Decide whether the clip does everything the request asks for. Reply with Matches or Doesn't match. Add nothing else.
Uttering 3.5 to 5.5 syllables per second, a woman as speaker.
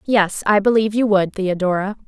Matches